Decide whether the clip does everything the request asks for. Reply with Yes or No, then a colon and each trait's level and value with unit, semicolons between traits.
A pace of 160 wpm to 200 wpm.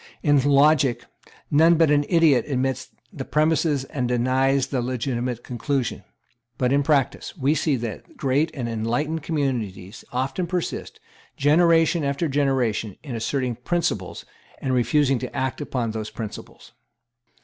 No: slow, 135 wpm